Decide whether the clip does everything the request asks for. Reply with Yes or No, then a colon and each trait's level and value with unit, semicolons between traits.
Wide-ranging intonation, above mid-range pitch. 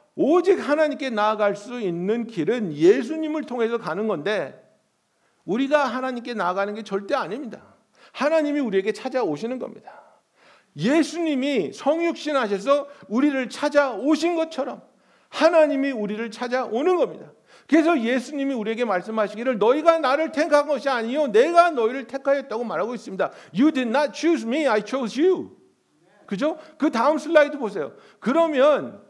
No: average, 4.8 semitones; very high, 275 Hz